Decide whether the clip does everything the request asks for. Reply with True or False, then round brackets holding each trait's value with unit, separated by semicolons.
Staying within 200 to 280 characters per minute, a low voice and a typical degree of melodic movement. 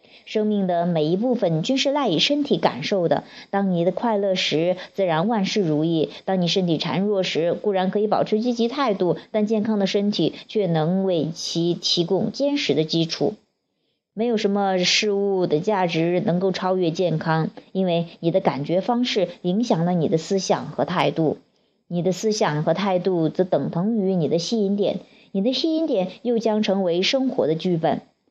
False (265 characters per minute; 190 Hz; 4.0 semitones)